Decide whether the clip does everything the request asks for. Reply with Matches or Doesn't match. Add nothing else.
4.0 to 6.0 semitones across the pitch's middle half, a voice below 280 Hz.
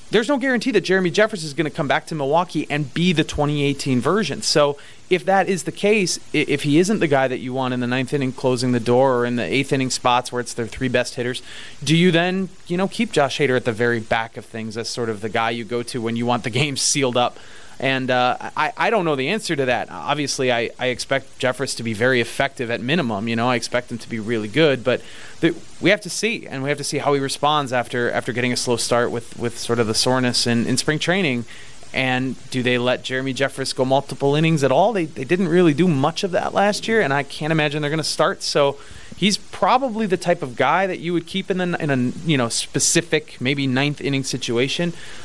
Matches